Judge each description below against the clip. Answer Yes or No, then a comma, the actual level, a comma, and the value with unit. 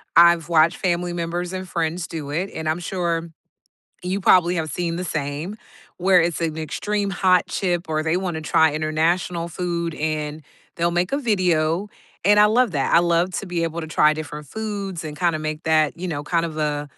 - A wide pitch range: No, narrow, 2.5 semitones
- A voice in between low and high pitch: Yes, medium, 170 Hz